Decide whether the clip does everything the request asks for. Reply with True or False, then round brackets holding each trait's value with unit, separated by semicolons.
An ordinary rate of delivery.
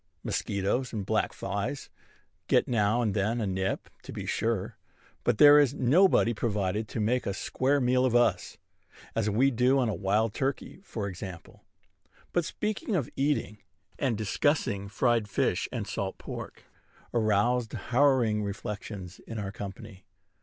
True (150 wpm)